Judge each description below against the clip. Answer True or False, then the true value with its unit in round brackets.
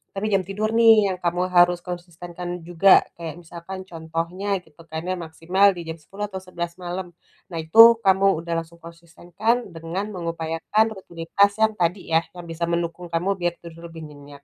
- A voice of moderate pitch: True (175 Hz)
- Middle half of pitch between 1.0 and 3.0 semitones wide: True (2.6 semitones)